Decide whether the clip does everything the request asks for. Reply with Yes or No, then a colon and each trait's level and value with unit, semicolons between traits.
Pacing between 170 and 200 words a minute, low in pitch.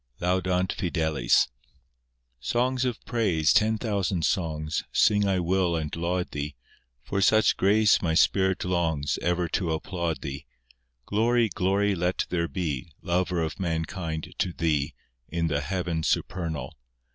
No: slow, 135 wpm; very low, 90 Hz